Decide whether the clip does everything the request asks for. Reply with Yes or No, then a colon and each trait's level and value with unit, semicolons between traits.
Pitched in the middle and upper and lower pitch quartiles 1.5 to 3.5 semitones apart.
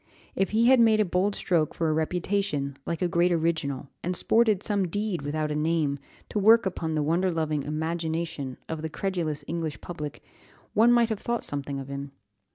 No: medium, 165 Hz; average, 4.6 semitones